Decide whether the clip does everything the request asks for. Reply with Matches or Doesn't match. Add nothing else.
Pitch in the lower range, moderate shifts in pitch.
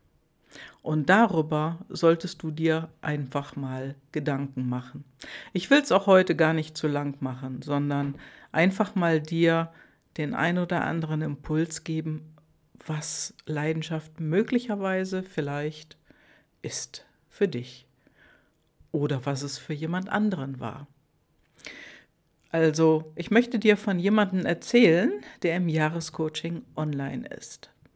Doesn't match